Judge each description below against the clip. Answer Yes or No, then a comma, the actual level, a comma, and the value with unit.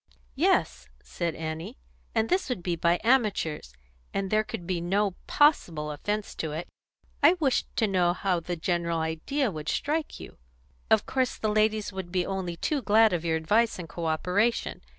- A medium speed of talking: Yes, average, 175 wpm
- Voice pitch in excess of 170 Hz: Yes, medium, 185 Hz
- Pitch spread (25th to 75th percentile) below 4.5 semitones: No, average, 4.8 semitones